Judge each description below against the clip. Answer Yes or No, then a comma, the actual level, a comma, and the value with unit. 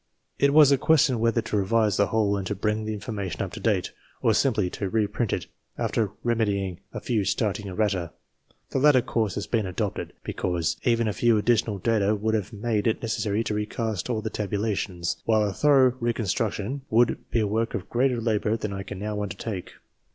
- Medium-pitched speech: No, low, 110 Hz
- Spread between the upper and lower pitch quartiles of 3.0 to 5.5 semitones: No, narrow, 2.4 semitones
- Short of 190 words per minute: No, average, 195 wpm